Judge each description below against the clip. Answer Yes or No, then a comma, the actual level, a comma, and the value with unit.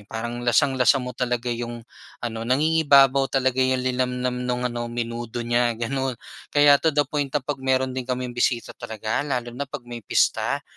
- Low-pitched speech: Yes, low, 125 Hz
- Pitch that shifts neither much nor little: No, narrow, 2.0 semitones